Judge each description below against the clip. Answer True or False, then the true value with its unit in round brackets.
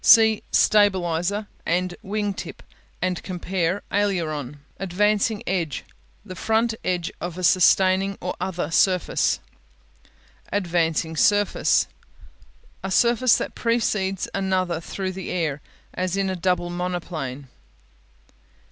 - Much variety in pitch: False (2.7 semitones)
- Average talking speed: False (110 wpm)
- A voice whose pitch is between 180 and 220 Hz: True (185 Hz)